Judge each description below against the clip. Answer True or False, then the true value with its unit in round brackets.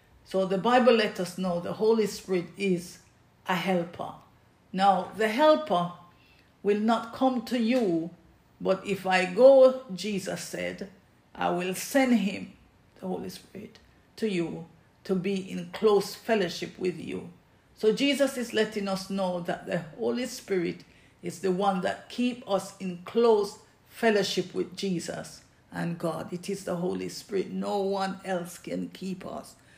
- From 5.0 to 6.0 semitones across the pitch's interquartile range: False (3.2 semitones)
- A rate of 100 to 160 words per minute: True (155 wpm)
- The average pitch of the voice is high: True (195 Hz)